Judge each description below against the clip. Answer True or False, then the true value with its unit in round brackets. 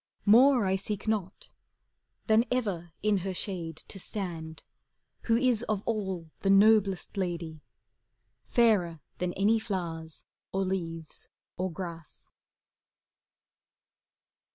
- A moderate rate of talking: False (105 wpm)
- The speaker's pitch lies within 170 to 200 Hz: True (190 Hz)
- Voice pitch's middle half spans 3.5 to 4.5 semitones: True (4.0 semitones)